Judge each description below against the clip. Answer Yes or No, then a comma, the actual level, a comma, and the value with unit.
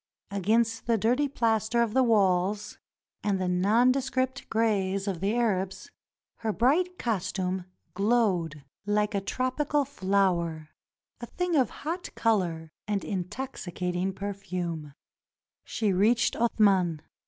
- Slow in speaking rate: Yes, slow, 120 wpm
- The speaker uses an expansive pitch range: No, average, 4.3 semitones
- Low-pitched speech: No, high, 205 Hz